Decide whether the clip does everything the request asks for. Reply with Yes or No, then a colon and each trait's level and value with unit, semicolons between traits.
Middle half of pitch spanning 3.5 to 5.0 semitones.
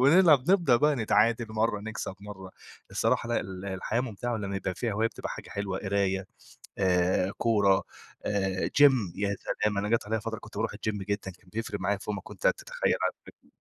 No: average, 3.1 semitones